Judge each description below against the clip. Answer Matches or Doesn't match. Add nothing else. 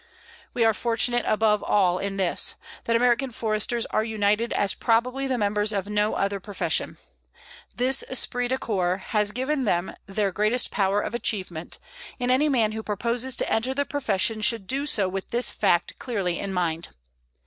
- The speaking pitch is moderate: Doesn't match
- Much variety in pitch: Doesn't match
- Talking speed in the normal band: Matches